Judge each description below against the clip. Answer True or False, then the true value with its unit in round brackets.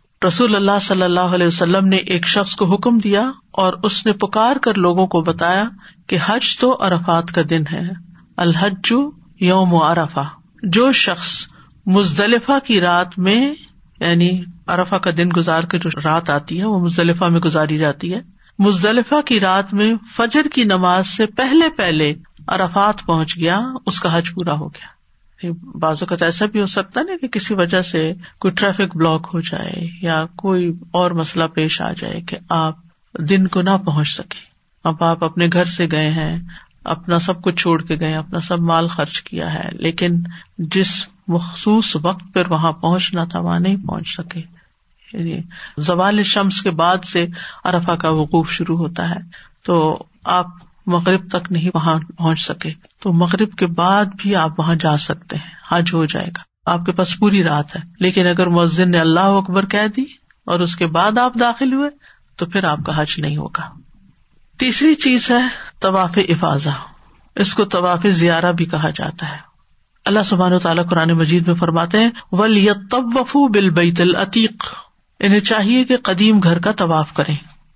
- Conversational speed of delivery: True (175 wpm)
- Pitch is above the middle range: False (180 Hz)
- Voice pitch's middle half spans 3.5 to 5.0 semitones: False (3.1 semitones)